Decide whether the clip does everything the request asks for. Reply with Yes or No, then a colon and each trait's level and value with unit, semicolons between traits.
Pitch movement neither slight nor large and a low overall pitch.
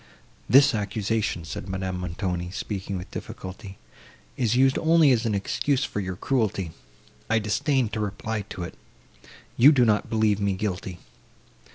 Yes: average, 3.8 semitones; low, 105 Hz